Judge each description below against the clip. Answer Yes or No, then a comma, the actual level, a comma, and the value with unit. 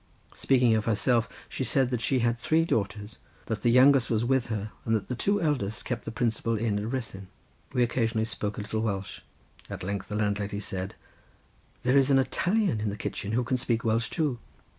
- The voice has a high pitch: No, low, 115 Hz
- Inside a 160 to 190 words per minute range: No, fast, 205 wpm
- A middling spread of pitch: Yes, average, 3.3 semitones